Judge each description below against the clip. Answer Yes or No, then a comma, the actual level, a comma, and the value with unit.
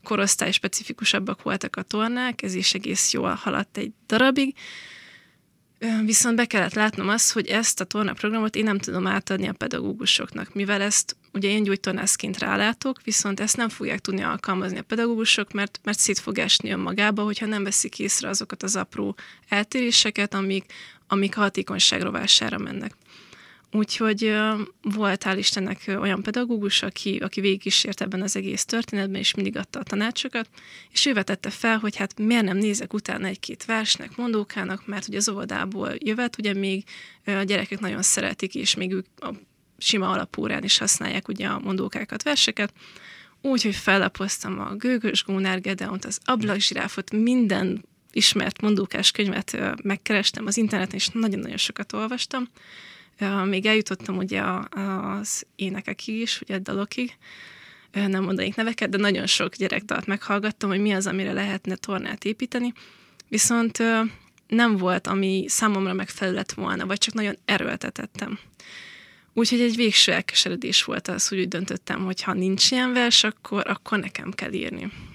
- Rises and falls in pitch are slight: Yes, narrow, 2.3 semitones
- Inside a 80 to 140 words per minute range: No, average, 150 wpm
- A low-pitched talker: No, high, 205 Hz